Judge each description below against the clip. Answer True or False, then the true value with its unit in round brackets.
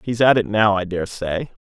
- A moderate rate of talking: False (220 wpm)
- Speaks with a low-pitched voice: True (105 Hz)